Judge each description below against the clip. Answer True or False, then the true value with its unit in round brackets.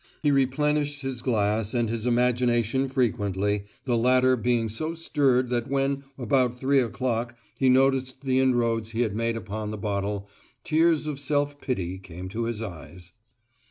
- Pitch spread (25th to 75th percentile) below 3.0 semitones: False (3.5 semitones)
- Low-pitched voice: True (125 Hz)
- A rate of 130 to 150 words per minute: False (160 wpm)